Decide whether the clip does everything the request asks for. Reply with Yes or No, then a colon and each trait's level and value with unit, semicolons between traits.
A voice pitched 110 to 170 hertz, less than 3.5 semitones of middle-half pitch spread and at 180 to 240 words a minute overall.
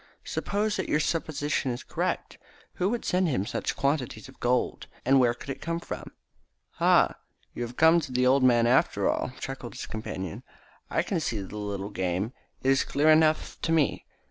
No: low, 135 Hz; average, 5.0 semitones; average, 195 wpm